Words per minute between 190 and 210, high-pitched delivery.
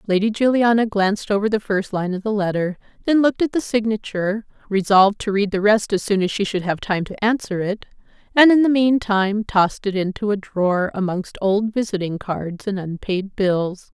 Yes: average, 195 wpm; high, 205 Hz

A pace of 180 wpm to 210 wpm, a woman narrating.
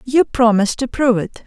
Yes: fast, 205 wpm; female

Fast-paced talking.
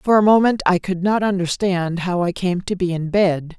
Yes: fast, 235 wpm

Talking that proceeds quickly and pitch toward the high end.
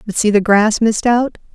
Yes: fast, 235 wpm; high, 220 Hz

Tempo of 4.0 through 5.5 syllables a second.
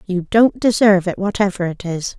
Yes: 5.4 syllables/s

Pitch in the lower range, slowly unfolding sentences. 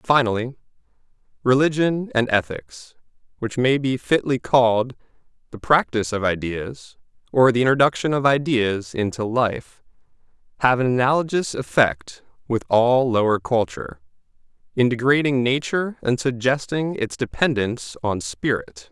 Yes: low, 120 Hz; slow, 110 wpm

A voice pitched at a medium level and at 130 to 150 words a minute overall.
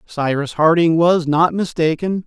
Yes: medium, 165 Hz; slow, 135 wpm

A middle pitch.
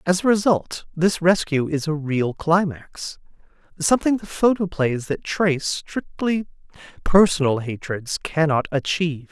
Yes: medium, 165 Hz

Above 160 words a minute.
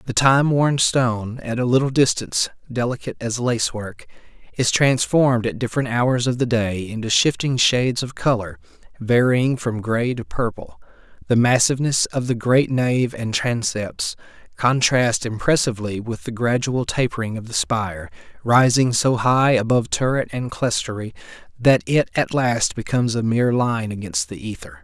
No: average, 155 wpm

